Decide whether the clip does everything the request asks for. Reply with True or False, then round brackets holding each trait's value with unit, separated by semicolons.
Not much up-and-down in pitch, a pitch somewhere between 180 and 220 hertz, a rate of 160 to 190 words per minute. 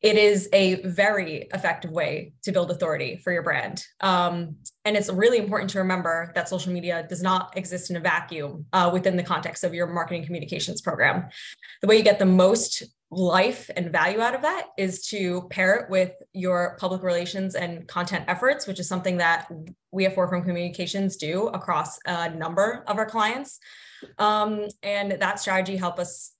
True (1.9 semitones; 185 Hz; 185 wpm)